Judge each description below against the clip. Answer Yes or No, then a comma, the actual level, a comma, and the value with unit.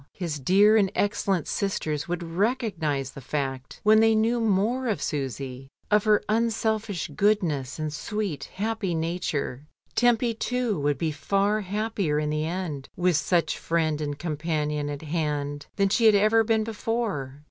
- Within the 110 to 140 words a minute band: No, average, 155 wpm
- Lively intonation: Yes, wide, 6.3 semitones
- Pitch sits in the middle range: Yes, medium, 180 Hz